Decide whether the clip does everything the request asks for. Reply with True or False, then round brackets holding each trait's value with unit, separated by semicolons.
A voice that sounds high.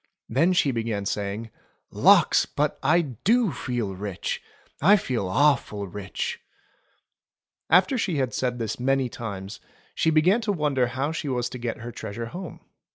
False (125 Hz)